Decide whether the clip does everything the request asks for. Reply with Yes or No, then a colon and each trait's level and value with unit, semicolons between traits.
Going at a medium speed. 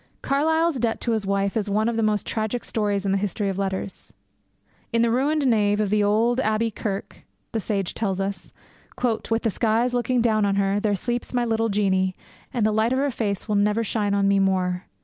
No: fast, 215 wpm